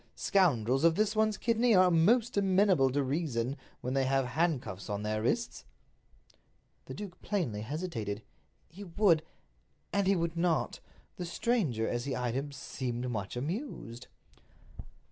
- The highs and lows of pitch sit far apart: Yes, wide, 7.9 semitones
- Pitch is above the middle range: No, medium, 155 Hz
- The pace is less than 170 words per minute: Yes, average, 140 wpm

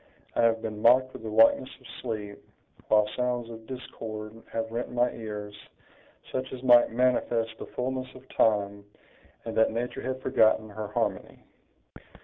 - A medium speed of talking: Yes, average, 155 wpm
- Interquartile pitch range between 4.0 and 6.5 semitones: No, narrow, 2.4 semitones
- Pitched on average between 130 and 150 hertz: No, low, 115 Hz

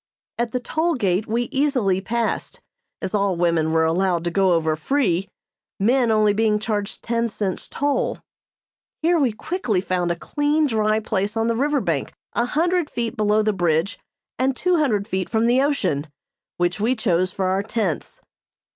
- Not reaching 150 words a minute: No, average, 175 wpm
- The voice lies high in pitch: Yes, high, 215 Hz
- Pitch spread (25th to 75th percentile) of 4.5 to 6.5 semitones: Yes, average, 5.3 semitones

